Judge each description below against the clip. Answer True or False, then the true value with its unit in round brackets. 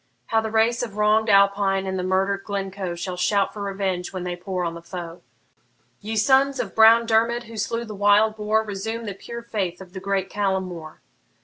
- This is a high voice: True (200 Hz)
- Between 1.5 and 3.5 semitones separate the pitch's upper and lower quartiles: True (2.7 semitones)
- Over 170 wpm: True (200 wpm)